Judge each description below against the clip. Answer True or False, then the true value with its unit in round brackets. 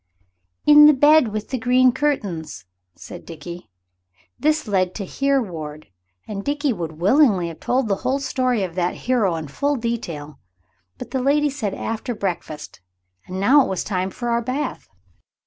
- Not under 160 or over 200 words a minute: True (165 wpm)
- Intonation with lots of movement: True (7.1 semitones)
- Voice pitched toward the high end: True (225 Hz)